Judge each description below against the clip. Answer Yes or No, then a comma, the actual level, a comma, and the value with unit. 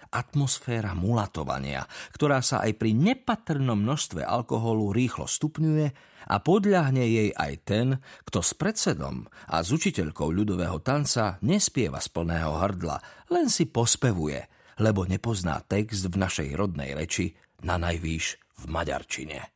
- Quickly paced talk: No, average, 130 wpm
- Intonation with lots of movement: Yes, wide, 7.9 semitones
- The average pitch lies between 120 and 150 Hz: No, low, 110 Hz